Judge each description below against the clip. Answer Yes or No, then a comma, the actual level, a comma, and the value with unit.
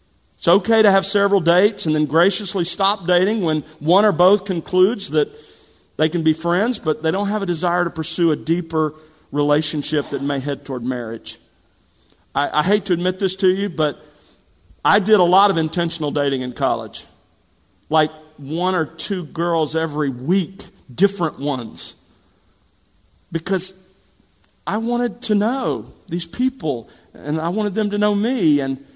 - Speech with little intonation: No, average, 5.2 semitones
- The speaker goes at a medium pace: Yes, average, 165 wpm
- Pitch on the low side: No, medium, 165 Hz